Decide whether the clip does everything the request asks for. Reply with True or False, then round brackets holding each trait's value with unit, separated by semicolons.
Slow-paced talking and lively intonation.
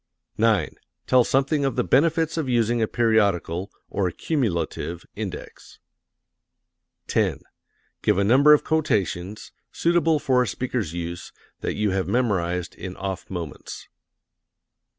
True (125 wpm; 6.4 semitones)